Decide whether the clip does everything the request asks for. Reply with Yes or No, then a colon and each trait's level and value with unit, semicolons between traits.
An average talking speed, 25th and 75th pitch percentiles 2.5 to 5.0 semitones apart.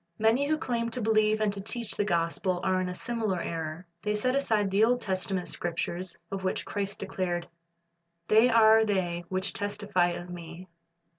Yes: average, 175 wpm; average, 3.4 semitones